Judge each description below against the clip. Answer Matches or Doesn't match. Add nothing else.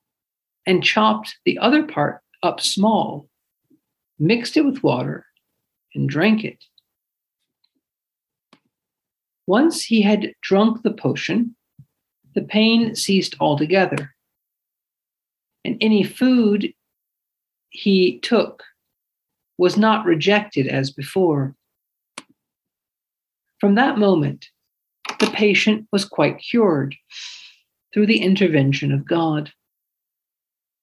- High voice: Matches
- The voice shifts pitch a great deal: Matches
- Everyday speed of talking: Doesn't match